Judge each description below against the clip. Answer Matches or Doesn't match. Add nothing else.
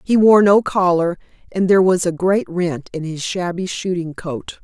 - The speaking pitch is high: Doesn't match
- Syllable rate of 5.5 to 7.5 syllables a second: Doesn't match